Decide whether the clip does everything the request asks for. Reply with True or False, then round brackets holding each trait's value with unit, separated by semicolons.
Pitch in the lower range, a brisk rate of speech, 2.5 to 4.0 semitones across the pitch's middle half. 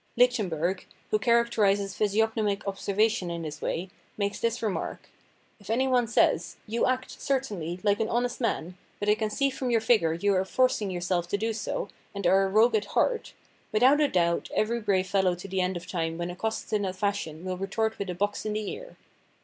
False (205 Hz; 210 wpm; 3.5 semitones)